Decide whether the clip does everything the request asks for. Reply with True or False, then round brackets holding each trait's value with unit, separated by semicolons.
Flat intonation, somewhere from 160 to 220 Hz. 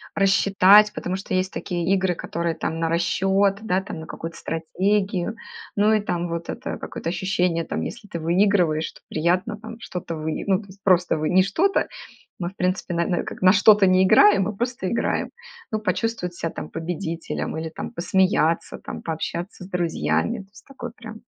False (3.1 semitones; 185 Hz)